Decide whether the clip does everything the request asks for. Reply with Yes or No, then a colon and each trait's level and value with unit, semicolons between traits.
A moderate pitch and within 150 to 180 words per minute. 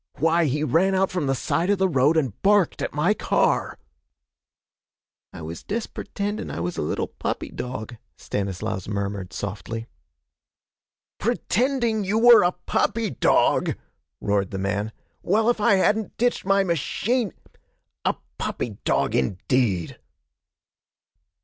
No: medium, 155 Hz; slow, 135 wpm